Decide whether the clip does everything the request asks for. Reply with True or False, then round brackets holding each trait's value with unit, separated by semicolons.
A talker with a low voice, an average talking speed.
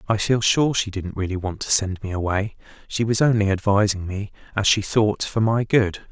False (105 Hz; 215 wpm)